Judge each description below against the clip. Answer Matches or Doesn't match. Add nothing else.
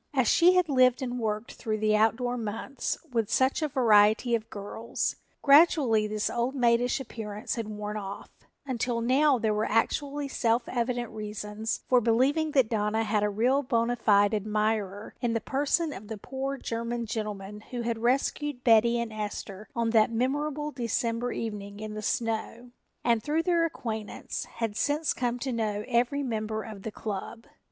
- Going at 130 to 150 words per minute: Doesn't match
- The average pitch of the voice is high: Matches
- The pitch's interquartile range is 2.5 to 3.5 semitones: Matches